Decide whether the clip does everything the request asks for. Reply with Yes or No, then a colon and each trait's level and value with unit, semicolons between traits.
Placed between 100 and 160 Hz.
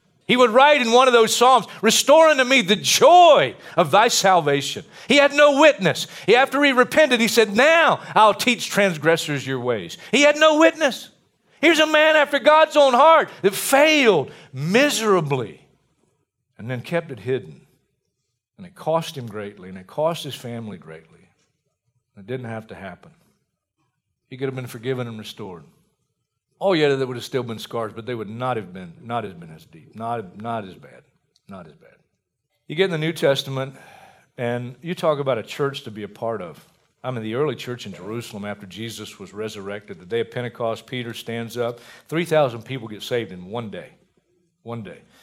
Yes: medium, 140 Hz